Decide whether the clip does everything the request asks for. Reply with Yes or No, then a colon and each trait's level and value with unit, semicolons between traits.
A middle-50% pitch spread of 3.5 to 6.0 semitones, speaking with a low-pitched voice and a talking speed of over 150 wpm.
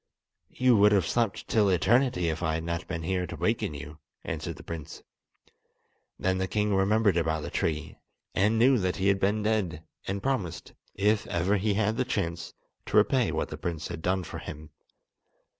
Yes: average, 4.1 semitones; very low, 95 Hz; average, 190 wpm